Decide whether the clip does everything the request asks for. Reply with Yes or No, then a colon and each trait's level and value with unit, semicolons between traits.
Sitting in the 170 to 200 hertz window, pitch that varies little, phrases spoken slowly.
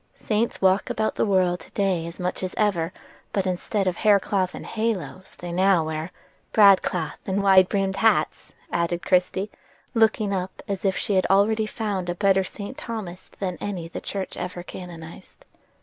No: high, 190 Hz; narrow, 2.2 semitones; average, 165 wpm